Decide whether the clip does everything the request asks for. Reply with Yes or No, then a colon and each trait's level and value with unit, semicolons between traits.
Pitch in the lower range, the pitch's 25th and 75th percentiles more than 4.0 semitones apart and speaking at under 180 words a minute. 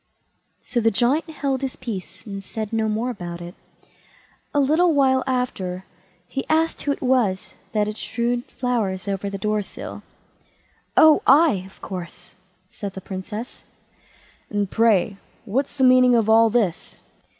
No: high, 225 Hz; average, 4.8 semitones; average, 150 wpm